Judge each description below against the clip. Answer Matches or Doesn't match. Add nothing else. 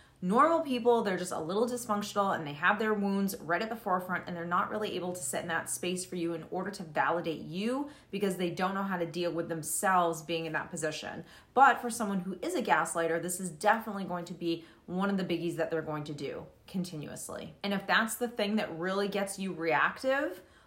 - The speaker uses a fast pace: Matches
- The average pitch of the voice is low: Doesn't match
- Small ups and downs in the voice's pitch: Doesn't match